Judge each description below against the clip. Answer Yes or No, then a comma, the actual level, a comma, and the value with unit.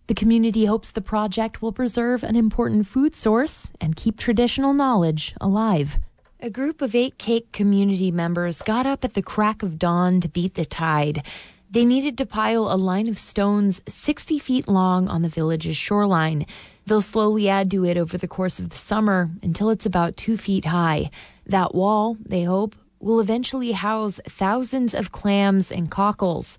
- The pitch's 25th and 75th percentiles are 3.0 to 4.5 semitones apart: Yes, average, 3.8 semitones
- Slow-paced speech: No, average, 175 wpm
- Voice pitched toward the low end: No, high, 205 Hz